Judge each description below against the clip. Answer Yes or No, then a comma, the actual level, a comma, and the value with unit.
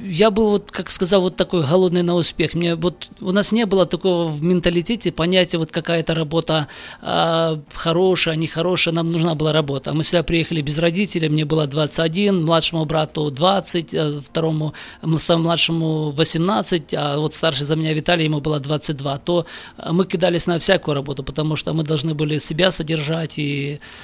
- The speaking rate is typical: No, fast, 170 wpm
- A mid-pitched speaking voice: Yes, medium, 165 Hz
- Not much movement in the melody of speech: Yes, narrow, 2.3 semitones